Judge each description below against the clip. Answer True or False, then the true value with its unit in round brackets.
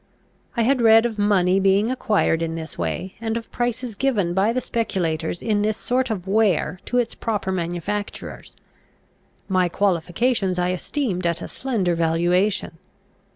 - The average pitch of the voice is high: True (200 Hz)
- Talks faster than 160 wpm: False (155 wpm)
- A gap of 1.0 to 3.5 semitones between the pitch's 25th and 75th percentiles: False (4.3 semitones)